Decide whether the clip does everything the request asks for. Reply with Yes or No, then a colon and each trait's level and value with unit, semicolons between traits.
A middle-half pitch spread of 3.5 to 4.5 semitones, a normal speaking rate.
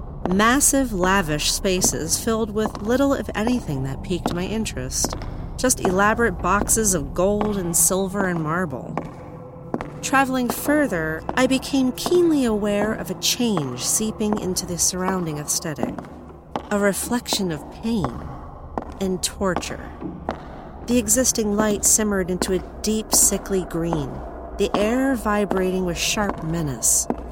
No: average, 3.9 semitones; slow, 125 wpm